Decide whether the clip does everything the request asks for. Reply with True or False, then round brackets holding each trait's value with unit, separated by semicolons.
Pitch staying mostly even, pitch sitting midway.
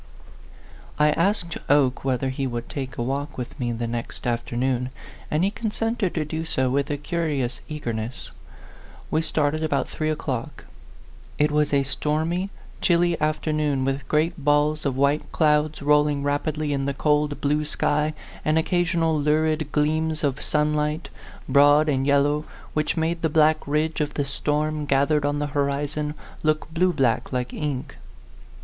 True (1.9 semitones; 150 Hz)